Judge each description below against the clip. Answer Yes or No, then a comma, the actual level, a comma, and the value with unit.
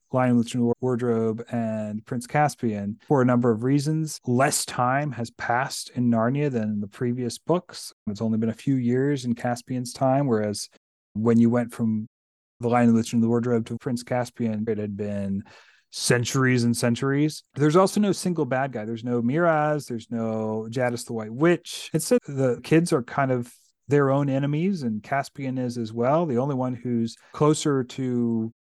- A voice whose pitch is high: No, low, 120 Hz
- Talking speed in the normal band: Yes, average, 180 wpm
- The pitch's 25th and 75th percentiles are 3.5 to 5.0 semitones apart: No, average, 3.1 semitones